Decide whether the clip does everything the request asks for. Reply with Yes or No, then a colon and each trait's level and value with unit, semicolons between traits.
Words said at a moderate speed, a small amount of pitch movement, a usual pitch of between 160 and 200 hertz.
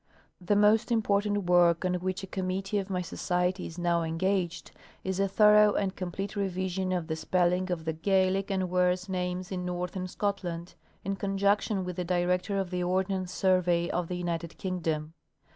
Yes: average, 180 wpm; narrow, 1.7 semitones; medium, 185 Hz